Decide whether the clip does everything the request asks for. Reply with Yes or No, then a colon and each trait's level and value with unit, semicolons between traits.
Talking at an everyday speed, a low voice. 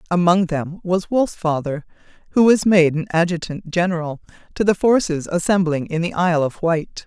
No: average, 160 wpm; medium, 175 Hz